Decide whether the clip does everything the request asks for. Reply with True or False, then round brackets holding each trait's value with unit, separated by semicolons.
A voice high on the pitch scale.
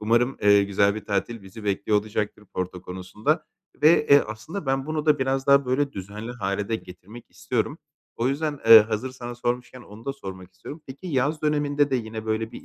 False (115 Hz)